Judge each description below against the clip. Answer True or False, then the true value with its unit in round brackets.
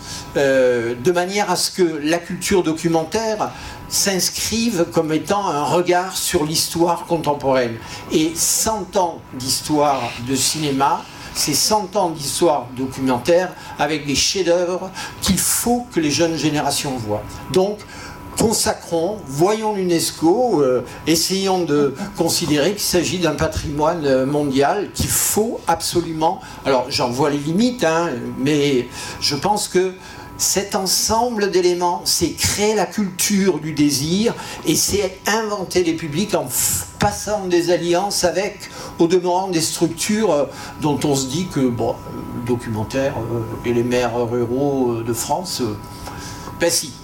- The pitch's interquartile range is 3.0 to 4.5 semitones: False (5.0 semitones)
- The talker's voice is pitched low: False (165 Hz)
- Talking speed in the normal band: False (130 wpm)